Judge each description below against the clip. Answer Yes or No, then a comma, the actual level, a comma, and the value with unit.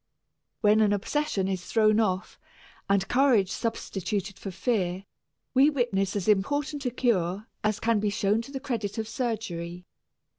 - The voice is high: Yes, high, 210 Hz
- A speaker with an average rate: Yes, average, 150 wpm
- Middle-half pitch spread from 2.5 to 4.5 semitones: Yes, average, 3.6 semitones